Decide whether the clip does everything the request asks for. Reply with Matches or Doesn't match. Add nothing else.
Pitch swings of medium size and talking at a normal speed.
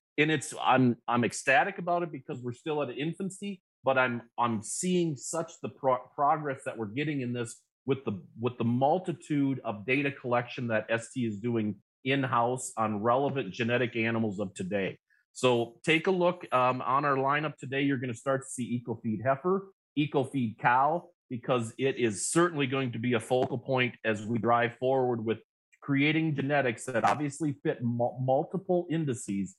Matches